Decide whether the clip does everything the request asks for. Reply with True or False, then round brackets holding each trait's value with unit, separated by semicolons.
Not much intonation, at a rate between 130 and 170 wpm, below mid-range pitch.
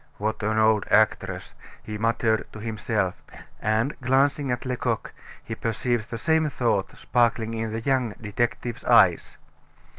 True (2.3 semitones; 140 wpm; 115 Hz)